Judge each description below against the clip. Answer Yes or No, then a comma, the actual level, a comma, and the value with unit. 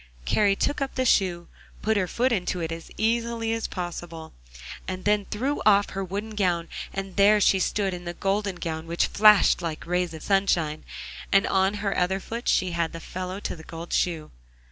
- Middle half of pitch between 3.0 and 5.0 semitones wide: Yes, average, 3.3 semitones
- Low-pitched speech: No, high, 190 Hz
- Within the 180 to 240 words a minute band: Yes, average, 195 wpm